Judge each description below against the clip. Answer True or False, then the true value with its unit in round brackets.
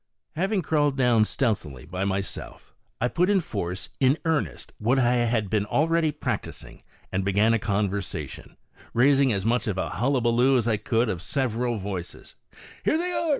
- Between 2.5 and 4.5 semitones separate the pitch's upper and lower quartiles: False (5.3 semitones)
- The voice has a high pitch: False (115 Hz)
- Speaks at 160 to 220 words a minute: True (165 wpm)